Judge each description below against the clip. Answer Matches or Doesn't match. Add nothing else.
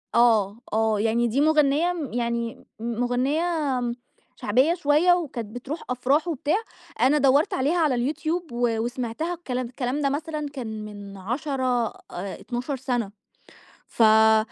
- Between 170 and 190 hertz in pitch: Doesn't match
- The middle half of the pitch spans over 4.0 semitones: Matches